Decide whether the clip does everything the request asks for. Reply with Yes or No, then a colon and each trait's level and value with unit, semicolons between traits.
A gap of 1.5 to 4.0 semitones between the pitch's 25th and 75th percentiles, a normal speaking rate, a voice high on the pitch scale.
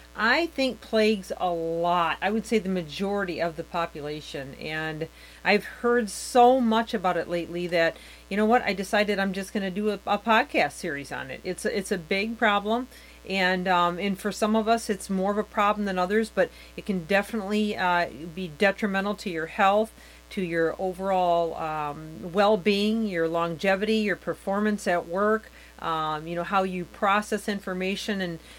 Yes: average, 3.5 semitones; average, 180 wpm; high, 195 Hz